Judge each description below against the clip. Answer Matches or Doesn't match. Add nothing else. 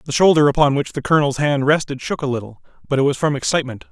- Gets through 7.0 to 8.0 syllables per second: Matches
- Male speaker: Matches